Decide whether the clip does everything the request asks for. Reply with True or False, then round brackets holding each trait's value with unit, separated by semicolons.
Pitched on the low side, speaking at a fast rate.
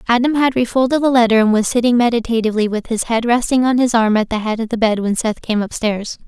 False (230 Hz; 250 wpm)